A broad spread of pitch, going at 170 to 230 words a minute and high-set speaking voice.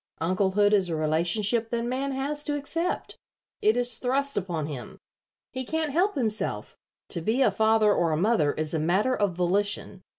Yes: wide, 6.8 semitones; average, 175 wpm; high, 215 Hz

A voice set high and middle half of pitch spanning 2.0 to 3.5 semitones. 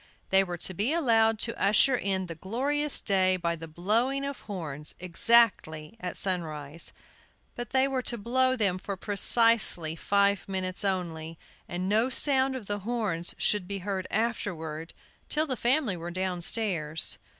No: high, 200 Hz; average, 5.2 semitones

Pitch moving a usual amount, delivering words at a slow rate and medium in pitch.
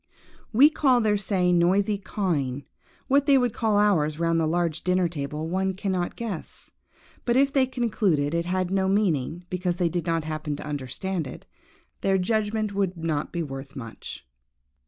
No: average, 4.6 semitones; average, 170 wpm; medium, 180 Hz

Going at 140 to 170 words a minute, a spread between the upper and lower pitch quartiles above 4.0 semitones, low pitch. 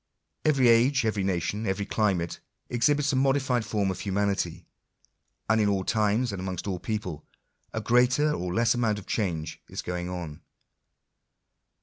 Yes: average, 155 wpm; average, 4.4 semitones; low, 105 Hz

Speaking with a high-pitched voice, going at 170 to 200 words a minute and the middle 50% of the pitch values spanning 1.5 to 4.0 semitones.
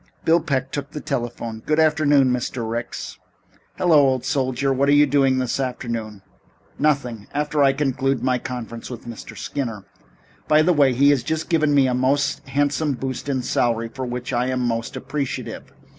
No: low, 135 Hz; average, 175 wpm; average, 2.8 semitones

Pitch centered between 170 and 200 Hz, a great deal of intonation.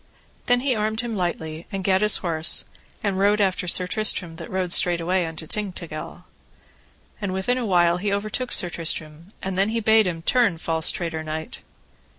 No: medium, 185 Hz; average, 4.1 semitones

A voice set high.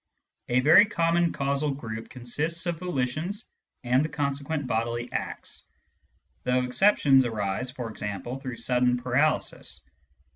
No: low, 130 Hz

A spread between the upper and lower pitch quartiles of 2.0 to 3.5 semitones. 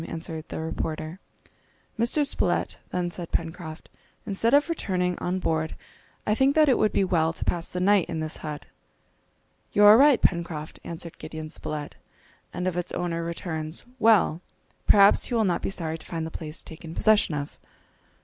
No: average, 4.2 semitones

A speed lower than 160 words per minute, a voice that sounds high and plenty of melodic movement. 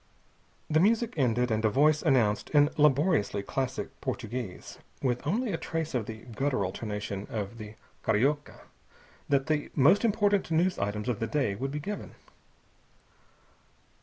No: average, 145 wpm; low, 135 Hz; wide, 6.2 semitones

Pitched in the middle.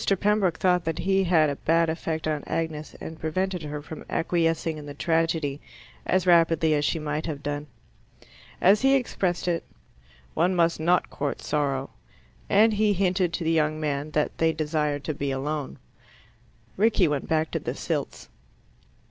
Yes: medium, 160 Hz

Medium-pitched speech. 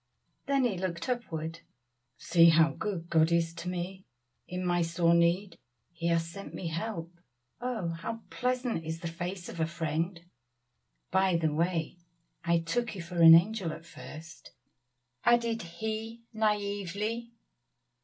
Yes: medium, 175 Hz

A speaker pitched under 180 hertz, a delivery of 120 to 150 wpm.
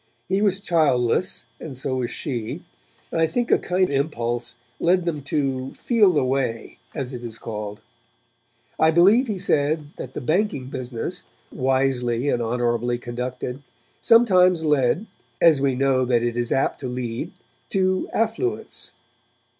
Yes: low, 135 Hz; average, 145 wpm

